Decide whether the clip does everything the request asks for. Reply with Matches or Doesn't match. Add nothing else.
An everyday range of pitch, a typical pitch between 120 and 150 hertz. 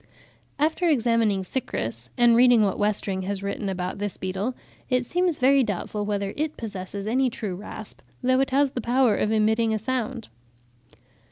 Doesn't match